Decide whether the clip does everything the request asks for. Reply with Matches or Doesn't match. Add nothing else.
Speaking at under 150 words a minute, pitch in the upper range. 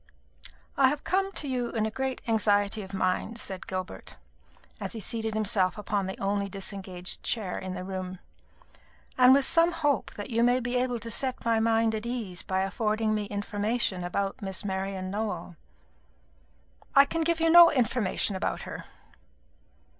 Doesn't match